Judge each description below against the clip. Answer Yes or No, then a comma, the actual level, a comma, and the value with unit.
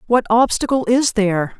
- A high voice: Yes, high, 225 Hz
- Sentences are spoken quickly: No, average, 150 wpm